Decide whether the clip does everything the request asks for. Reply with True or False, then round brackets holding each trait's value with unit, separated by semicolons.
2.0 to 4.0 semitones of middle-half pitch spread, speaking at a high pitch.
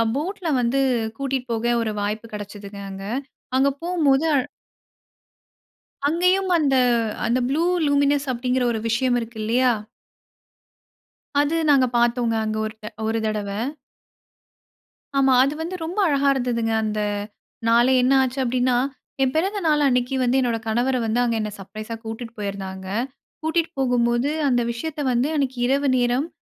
True (3.7 semitones; 250 Hz)